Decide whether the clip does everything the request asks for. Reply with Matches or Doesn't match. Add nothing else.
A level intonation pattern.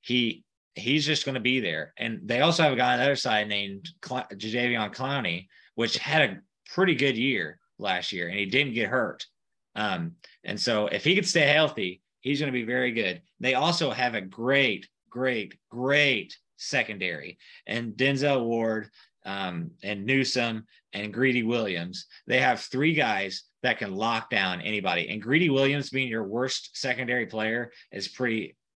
Doesn't match